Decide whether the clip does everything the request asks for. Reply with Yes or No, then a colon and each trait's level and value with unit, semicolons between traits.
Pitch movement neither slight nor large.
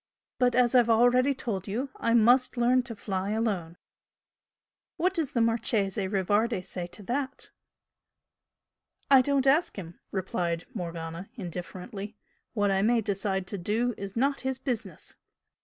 Yes: average, 4.5 semitones